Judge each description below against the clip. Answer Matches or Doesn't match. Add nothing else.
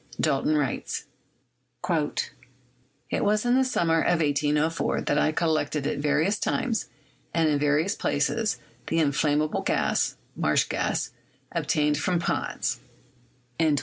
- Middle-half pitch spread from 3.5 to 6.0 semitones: Doesn't match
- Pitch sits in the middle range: Matches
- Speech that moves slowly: Matches